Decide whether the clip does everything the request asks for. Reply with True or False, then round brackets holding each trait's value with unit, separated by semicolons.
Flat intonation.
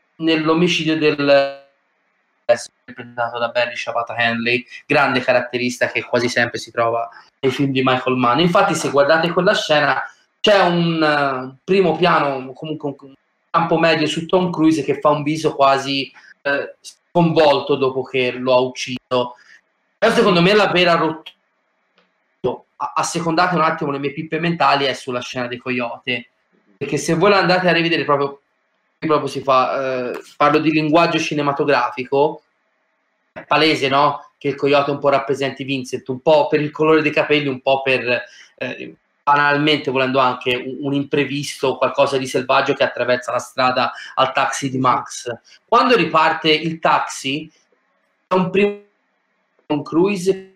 False (3.4 semitones)